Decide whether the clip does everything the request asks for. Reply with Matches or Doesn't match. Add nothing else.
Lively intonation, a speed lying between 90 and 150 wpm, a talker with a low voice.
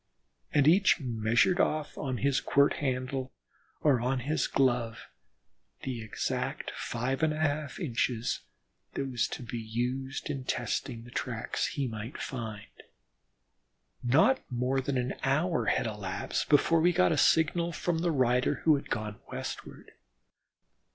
Doesn't match